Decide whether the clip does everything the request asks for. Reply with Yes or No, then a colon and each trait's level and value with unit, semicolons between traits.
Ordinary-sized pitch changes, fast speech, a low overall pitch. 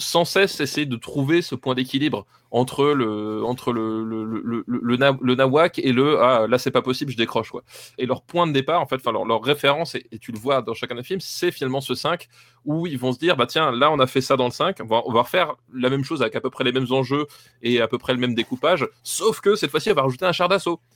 Yes: average, 3.5 semitones; fast, 280 wpm; low, 130 Hz